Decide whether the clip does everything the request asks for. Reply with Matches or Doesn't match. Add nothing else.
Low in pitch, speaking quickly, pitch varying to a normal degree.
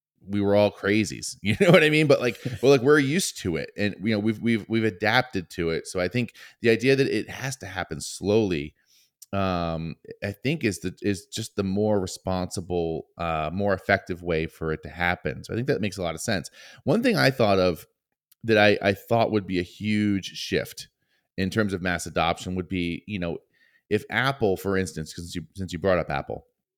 Matches